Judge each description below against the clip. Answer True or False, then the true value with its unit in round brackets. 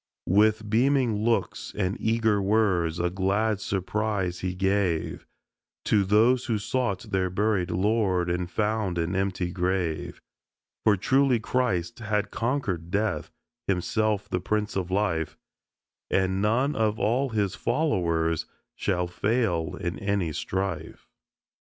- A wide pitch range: False (3.4 semitones)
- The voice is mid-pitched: False (100 Hz)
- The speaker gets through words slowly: True (125 wpm)